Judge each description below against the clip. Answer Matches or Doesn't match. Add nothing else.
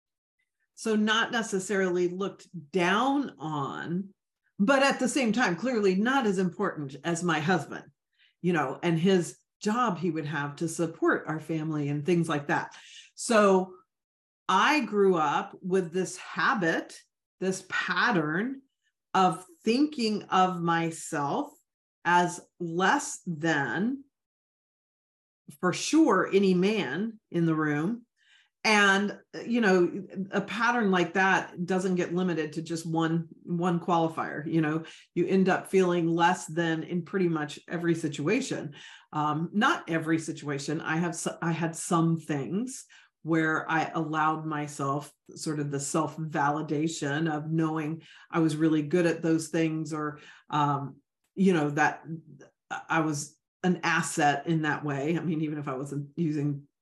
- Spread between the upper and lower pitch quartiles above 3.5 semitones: Doesn't match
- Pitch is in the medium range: Matches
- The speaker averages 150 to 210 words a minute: Doesn't match